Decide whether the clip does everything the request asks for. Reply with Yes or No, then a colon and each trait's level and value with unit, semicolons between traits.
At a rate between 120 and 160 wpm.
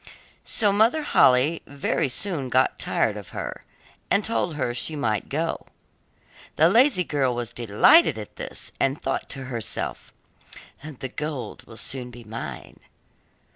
Yes: average, 140 wpm